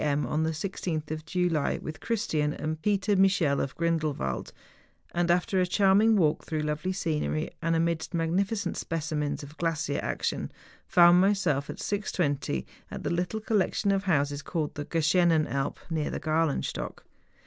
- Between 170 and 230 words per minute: No, average, 155 wpm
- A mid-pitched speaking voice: Yes, medium, 165 Hz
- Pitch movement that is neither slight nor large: Yes, average, 3.5 semitones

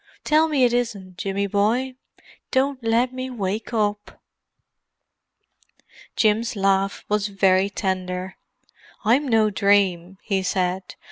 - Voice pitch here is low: No, high, 205 Hz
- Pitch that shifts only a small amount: No, average, 3.8 semitones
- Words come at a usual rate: No, slow, 115 wpm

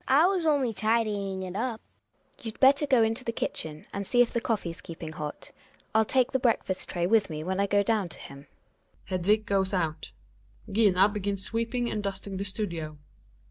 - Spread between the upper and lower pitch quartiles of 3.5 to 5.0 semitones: Yes, average, 3.9 semitones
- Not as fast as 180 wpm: No, average, 190 wpm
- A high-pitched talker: Yes, high, 205 Hz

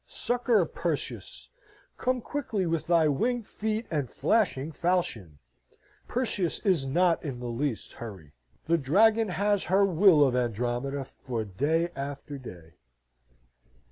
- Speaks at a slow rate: Yes, slow, 125 wpm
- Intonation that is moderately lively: No, wide, 7.3 semitones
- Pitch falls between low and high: Yes, medium, 160 Hz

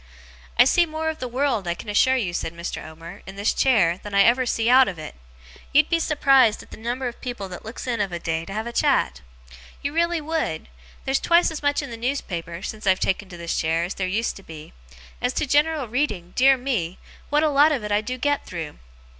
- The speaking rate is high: Yes, fast, 240 wpm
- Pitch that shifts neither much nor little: No, wide, 7.0 semitones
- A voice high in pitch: Yes, high, 235 Hz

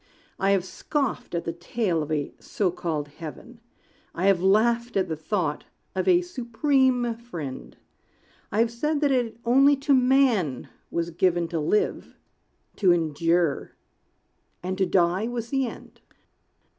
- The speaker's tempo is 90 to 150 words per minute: Yes, average, 145 wpm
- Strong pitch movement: Yes, wide, 6.4 semitones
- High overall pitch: Yes, high, 200 Hz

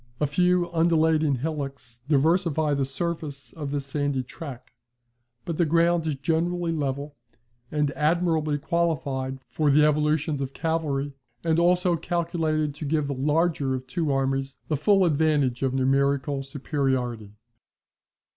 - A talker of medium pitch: Yes, medium, 150 Hz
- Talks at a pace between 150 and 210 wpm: No, slow, 135 wpm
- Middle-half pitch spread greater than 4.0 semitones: No, average, 3.0 semitones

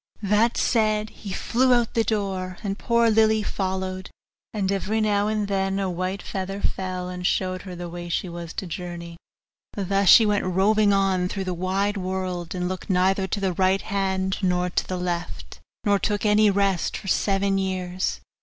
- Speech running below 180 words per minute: No, average, 185 wpm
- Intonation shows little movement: Yes, narrow, 2.0 semitones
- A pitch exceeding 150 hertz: Yes, high, 190 Hz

